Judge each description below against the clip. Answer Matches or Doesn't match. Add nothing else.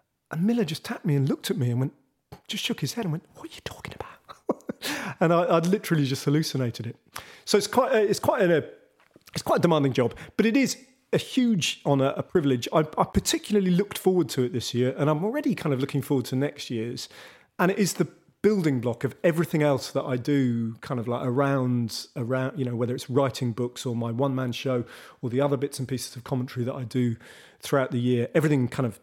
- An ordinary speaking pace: Doesn't match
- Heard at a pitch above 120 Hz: Matches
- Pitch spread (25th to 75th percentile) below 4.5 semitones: Doesn't match